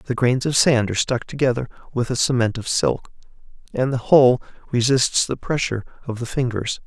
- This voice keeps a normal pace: Yes, average, 185 wpm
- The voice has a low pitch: Yes, low, 125 Hz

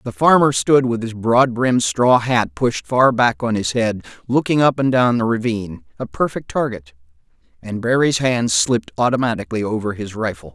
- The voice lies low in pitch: Yes, low, 115 Hz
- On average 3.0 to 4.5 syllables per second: No, 5.1 syllables/s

